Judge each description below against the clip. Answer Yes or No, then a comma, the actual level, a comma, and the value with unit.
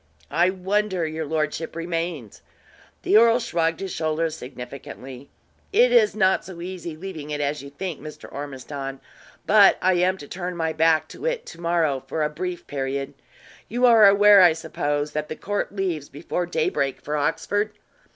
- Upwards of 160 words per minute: Yes, average, 170 wpm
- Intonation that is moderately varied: Yes, average, 4.4 semitones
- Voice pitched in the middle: Yes, medium, 165 Hz